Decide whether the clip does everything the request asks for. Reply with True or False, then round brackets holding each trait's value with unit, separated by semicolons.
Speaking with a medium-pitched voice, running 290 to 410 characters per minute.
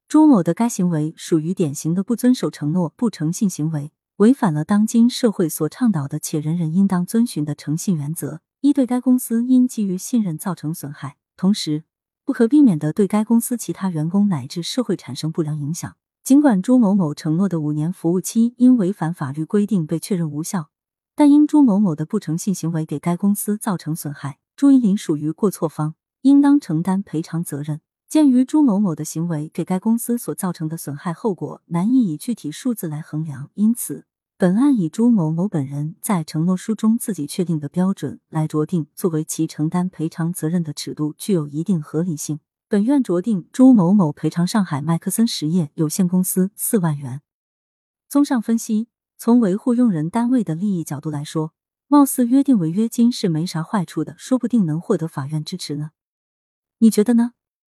True (180 Hz; 295 characters per minute)